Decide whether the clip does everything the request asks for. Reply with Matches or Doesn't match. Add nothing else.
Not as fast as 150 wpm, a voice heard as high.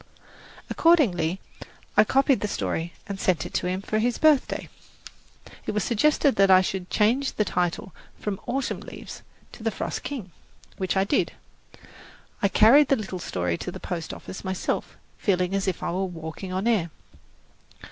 Doesn't match